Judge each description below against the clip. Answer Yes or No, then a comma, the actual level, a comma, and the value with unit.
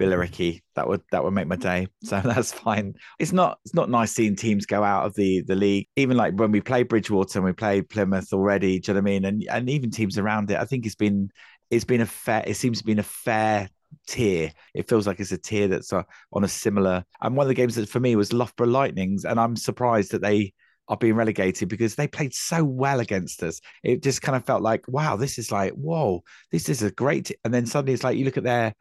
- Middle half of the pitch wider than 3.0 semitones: Yes, average, 3.8 semitones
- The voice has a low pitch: Yes, low, 110 Hz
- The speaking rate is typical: No, fast, 260 wpm